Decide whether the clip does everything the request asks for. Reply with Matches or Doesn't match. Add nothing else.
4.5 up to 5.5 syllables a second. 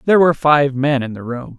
Doesn't match